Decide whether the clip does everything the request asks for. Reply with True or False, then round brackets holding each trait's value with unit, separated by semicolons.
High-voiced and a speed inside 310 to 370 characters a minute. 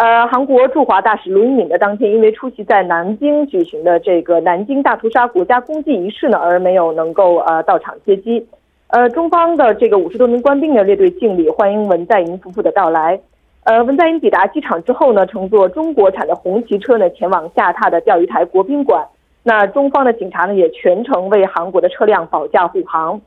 True (225 Hz; 325 characters per minute)